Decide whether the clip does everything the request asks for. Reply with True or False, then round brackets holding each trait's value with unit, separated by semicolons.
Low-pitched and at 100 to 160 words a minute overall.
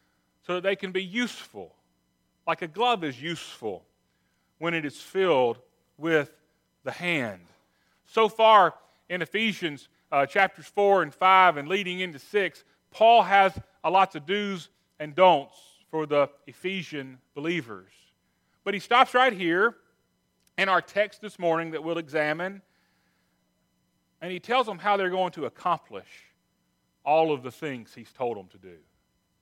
False (170 Hz; 150 wpm)